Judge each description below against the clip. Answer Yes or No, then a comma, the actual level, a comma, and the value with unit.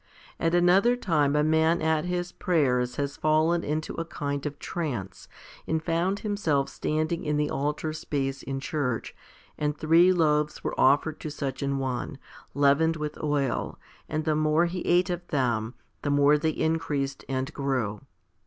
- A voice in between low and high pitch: Yes, medium, 150 Hz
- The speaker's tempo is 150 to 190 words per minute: Yes, average, 160 wpm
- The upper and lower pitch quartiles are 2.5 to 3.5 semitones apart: Yes, average, 2.8 semitones